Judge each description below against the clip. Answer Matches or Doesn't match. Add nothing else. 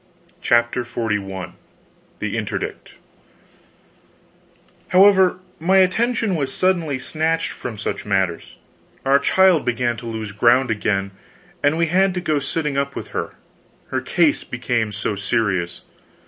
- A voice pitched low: Matches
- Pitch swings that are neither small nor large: Doesn't match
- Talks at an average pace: Doesn't match